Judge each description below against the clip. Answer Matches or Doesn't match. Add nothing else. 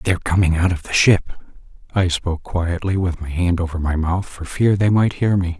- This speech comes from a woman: Doesn't match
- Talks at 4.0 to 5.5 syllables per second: Matches